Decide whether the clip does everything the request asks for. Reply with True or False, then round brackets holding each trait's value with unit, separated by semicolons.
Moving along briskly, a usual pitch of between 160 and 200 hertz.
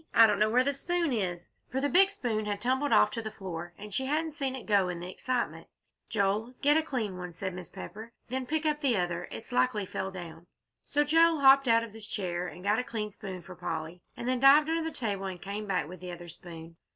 False (255 wpm; 215 Hz)